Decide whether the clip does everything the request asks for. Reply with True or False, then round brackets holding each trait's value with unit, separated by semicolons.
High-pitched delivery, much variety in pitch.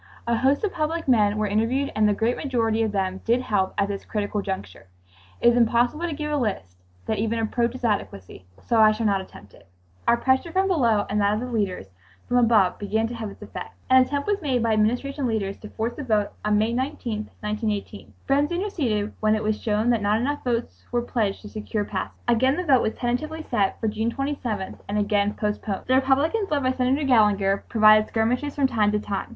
False (225 Hz; 3.8 semitones)